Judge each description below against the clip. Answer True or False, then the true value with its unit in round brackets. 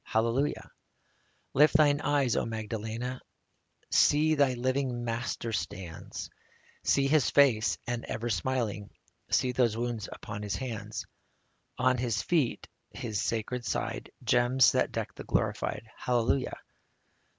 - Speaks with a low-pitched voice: True (120 Hz)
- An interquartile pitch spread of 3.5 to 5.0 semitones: False (2.9 semitones)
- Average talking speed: False (130 wpm)